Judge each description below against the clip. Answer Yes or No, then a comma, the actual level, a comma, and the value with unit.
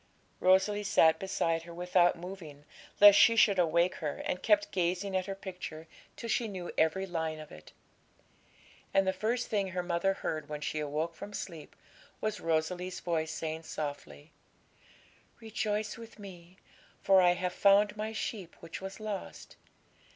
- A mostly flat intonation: No, average, 3.6 semitones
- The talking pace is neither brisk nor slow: Yes, average, 160 wpm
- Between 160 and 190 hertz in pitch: Yes, medium, 185 Hz